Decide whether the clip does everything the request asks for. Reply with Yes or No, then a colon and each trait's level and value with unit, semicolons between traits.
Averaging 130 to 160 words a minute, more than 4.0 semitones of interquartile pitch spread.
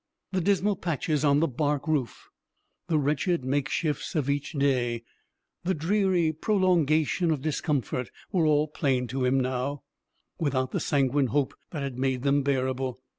No: average, 150 wpm; average, 3.4 semitones